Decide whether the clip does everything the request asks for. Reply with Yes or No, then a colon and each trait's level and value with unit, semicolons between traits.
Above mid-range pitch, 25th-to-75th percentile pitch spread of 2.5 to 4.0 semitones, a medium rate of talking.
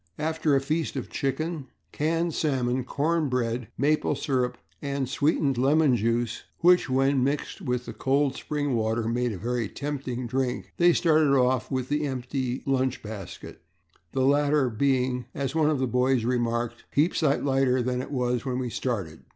No: low, 130 Hz; average, 2.8 semitones; average, 165 wpm